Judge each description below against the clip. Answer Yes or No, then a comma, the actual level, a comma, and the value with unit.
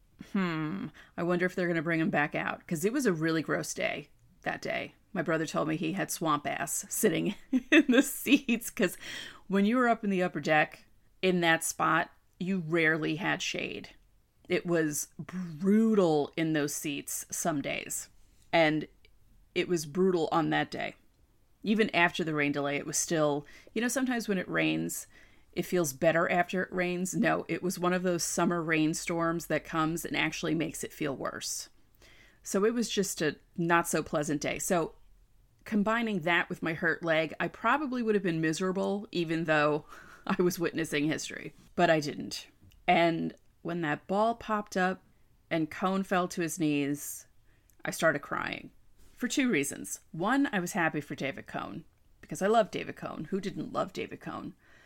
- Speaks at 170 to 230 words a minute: Yes, average, 180 wpm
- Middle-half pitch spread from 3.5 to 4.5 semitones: Yes, average, 3.8 semitones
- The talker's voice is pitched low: No, medium, 170 Hz